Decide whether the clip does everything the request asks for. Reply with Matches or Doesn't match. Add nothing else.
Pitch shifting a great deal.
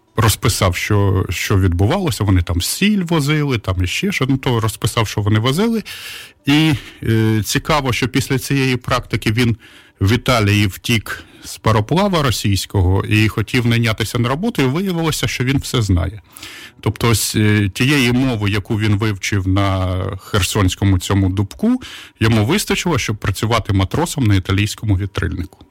Doesn't match